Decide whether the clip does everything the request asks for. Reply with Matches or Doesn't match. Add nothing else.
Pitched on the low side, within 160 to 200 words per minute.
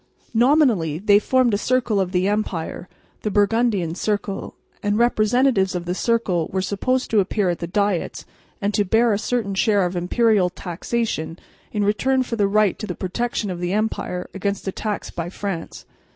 Doesn't match